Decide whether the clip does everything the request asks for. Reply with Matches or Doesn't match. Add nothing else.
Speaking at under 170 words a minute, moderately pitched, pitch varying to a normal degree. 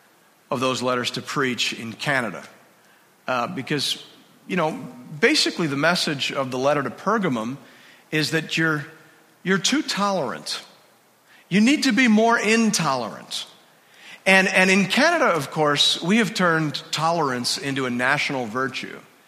Doesn't match